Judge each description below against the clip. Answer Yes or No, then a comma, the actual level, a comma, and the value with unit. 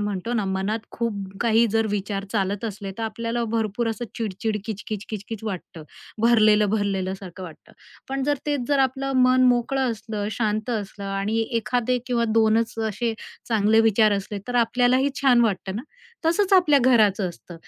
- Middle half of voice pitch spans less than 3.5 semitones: Yes, average, 2.9 semitones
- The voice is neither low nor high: No, high, 220 Hz